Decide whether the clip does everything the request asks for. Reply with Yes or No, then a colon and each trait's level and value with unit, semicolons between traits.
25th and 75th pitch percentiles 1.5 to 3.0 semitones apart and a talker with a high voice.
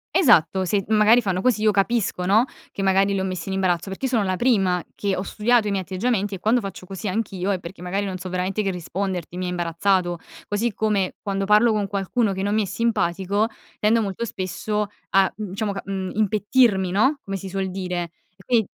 Yes: narrow, 2.4 semitones; high, 195 Hz